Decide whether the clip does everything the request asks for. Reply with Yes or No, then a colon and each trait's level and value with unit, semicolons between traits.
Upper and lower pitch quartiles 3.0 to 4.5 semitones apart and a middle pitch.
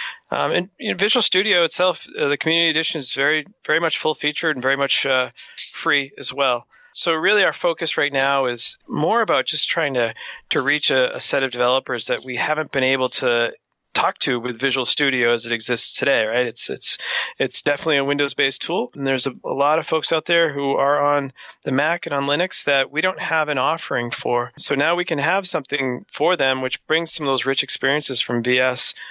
Yes: average, 3.4 semitones; medium, 145 Hz